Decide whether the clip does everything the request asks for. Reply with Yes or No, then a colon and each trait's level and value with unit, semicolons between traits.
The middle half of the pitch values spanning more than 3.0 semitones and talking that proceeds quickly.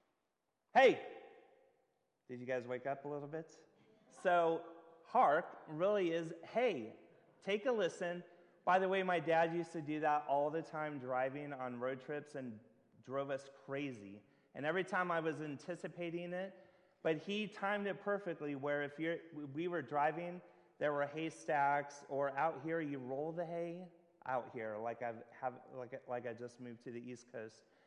No: average, 4.3 semitones; average, 170 wpm